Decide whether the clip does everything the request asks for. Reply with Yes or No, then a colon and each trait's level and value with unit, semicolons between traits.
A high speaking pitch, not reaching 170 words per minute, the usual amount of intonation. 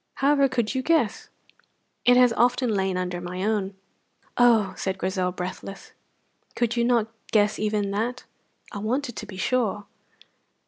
Yes: high, 215 Hz; average, 145 wpm; average, 4.2 semitones